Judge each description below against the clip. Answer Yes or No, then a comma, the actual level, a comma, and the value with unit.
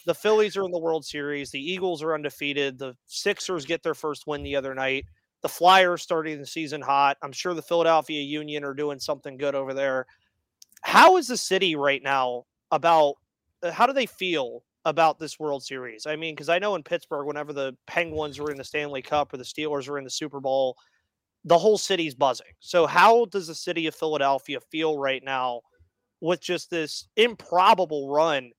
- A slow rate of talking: No, average, 195 wpm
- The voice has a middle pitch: Yes, medium, 150 Hz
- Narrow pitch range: No, average, 3.6 semitones